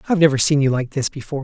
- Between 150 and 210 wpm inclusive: No, fast, 290 wpm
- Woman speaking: No, male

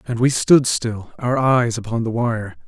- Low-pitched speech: Yes, low, 120 Hz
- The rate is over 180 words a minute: Yes, average, 200 wpm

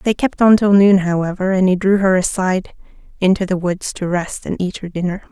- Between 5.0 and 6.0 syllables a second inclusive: Yes, 5.5 syllables/s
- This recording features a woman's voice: Yes, female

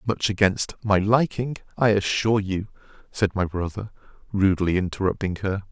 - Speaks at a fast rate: No, slow, 135 wpm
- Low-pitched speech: Yes, low, 100 Hz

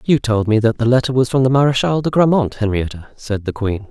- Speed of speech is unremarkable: No, fast, 245 wpm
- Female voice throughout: No, male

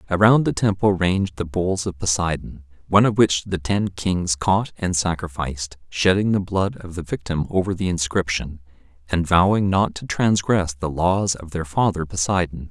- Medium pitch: No, very low, 90 Hz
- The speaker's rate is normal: Yes, average, 175 wpm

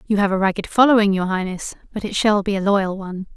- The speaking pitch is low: No, high, 200 Hz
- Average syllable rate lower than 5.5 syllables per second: No, 6.4 syllables/s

